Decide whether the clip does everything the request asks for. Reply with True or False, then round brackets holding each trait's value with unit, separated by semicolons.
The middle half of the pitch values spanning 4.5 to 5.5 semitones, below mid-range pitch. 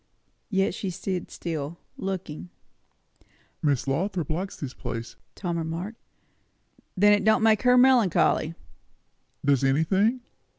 False (5.0 semitones; 180 Hz)